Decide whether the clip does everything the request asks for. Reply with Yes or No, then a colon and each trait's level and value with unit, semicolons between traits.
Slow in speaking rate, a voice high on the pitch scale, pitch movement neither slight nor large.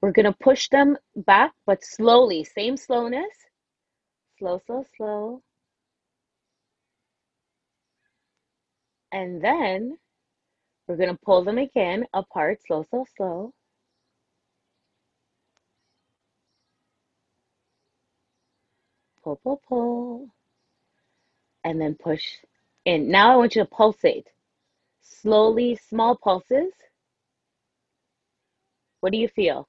Yes: slow, 85 wpm; high, 225 Hz; average, 4.8 semitones